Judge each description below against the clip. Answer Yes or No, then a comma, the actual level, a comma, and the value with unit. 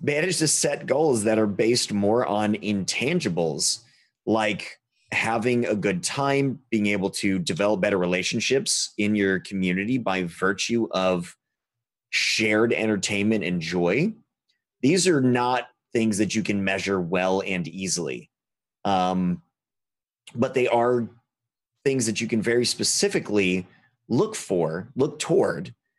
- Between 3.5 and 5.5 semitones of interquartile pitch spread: Yes, average, 3.9 semitones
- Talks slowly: Yes, slow, 130 wpm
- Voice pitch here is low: Yes, low, 110 Hz